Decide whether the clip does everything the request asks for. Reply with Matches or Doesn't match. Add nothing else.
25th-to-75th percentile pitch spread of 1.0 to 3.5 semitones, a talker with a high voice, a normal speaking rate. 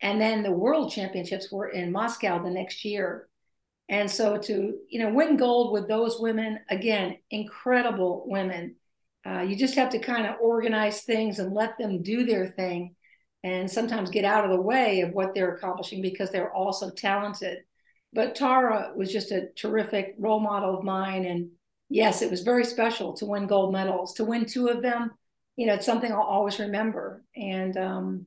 Matches